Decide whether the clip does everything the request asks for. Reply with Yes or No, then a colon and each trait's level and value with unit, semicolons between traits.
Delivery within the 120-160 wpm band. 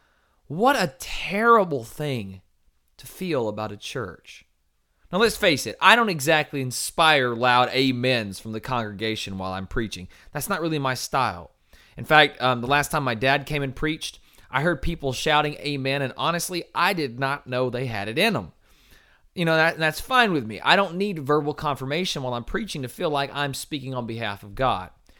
No: average, 195 wpm